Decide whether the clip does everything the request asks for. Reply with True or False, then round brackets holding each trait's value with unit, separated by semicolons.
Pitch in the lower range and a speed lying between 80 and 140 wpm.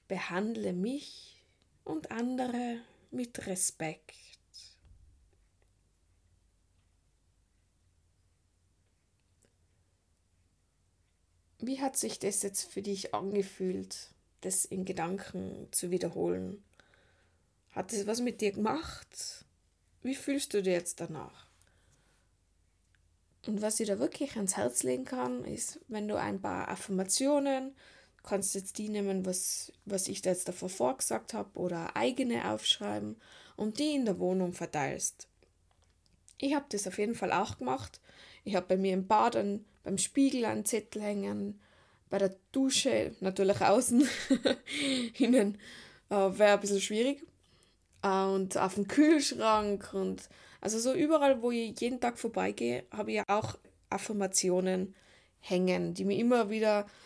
False (190 Hz; 125 wpm)